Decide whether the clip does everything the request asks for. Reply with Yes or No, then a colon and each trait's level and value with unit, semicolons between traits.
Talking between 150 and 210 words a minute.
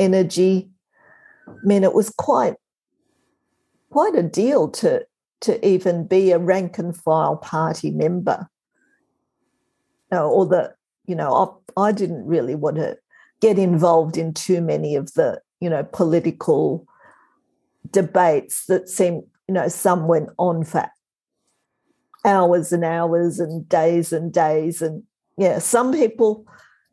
No: slow, 135 wpm